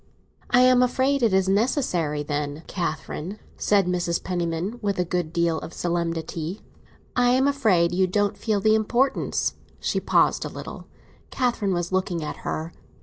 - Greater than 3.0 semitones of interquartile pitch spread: Yes, average, 5.0 semitones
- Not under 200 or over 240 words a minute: No, average, 155 wpm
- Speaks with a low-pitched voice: No, medium, 185 Hz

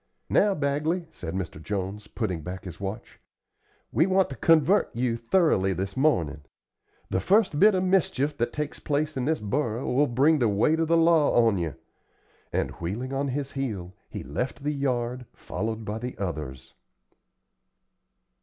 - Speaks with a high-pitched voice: No, low, 125 Hz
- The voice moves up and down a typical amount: No, wide, 7.5 semitones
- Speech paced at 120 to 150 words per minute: No, average, 165 wpm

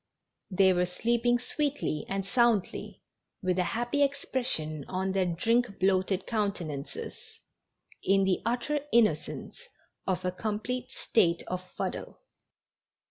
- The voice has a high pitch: Yes, high, 195 Hz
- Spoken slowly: Yes, slow, 115 wpm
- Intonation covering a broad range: No, average, 4.8 semitones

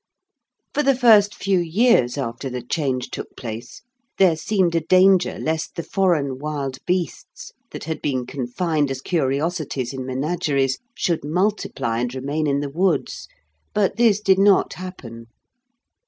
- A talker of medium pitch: Yes, medium, 155 Hz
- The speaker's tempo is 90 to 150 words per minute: Yes, average, 145 wpm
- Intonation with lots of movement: Yes, wide, 5.8 semitones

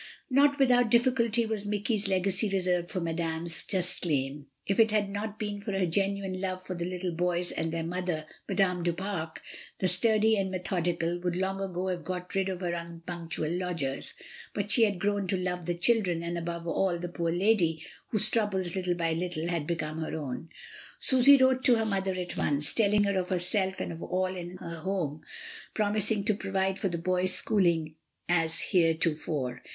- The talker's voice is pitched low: No, medium, 185 Hz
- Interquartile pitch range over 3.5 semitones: No, average, 2.9 semitones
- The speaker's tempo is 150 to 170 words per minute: No, average, 190 wpm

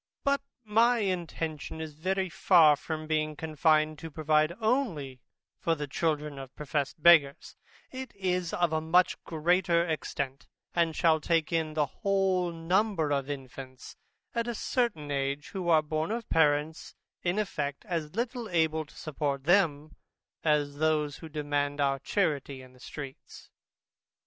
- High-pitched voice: No, medium, 155 Hz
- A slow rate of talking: No, average, 150 wpm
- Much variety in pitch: No, average, 3.5 semitones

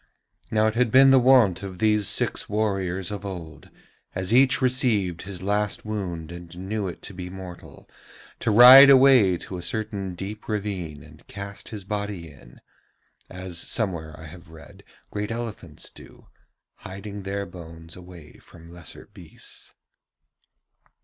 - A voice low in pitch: Yes, very low, 95 Hz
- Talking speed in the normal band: Yes, average, 150 wpm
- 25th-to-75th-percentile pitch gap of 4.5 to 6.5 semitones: No, average, 3.5 semitones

